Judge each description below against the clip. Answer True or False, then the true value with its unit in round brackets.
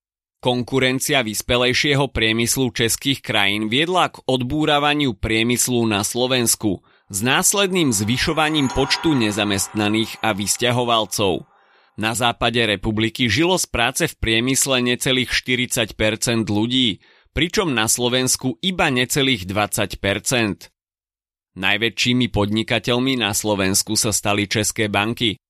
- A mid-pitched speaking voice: False (115 Hz)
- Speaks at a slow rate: True (100 wpm)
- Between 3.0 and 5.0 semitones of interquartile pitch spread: True (3.5 semitones)